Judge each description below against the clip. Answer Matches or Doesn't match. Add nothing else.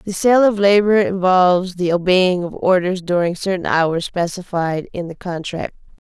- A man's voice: Doesn't match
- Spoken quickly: Doesn't match